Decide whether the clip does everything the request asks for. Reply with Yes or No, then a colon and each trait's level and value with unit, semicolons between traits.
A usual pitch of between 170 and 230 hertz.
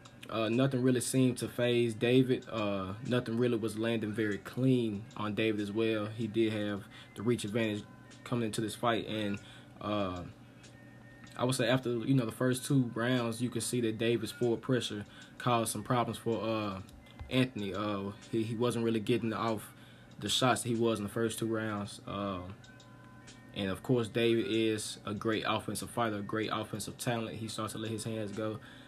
No: low, 115 Hz